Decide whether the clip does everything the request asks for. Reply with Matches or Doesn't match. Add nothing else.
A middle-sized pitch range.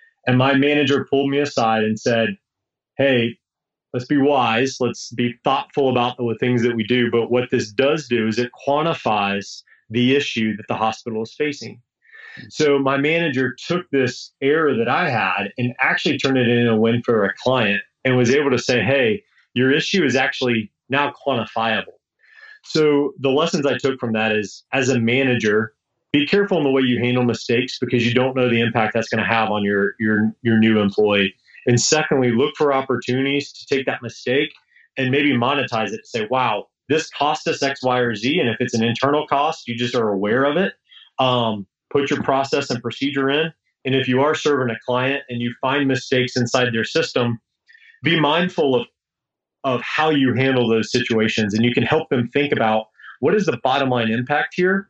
Matches